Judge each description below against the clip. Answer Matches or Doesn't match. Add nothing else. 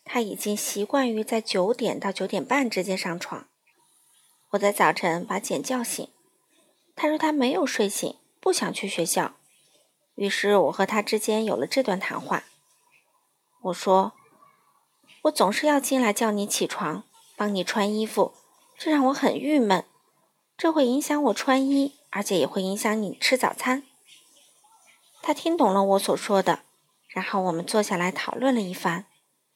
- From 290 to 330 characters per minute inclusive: Doesn't match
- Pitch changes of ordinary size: Doesn't match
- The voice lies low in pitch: Doesn't match